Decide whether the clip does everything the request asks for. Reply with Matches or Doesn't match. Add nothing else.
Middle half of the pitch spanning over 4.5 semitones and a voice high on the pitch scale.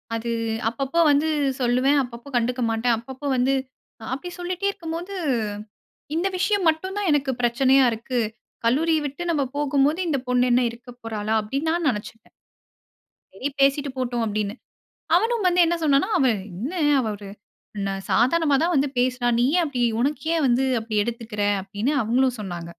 Matches